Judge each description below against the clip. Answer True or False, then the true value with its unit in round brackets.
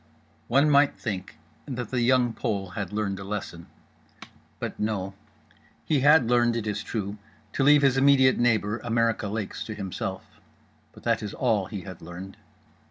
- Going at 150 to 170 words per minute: True (165 wpm)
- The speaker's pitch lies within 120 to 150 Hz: False (110 Hz)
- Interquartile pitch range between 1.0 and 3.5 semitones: False (4.2 semitones)